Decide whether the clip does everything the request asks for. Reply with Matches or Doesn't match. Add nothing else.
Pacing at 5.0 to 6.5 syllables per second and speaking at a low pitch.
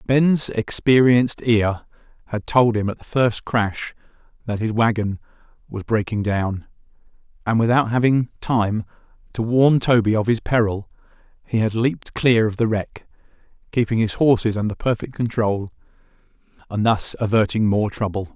Doesn't match